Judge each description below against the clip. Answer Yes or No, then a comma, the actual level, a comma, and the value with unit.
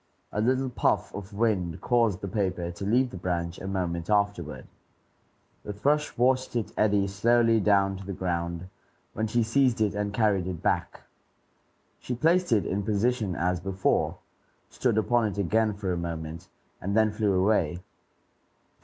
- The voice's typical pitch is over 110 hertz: No, low, 100 Hz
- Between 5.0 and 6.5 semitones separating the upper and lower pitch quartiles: No, average, 3.6 semitones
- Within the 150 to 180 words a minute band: Yes, average, 160 wpm